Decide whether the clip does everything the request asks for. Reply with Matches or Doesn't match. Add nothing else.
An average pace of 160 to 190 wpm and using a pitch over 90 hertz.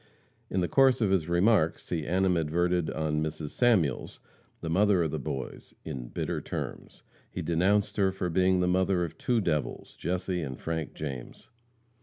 Doesn't match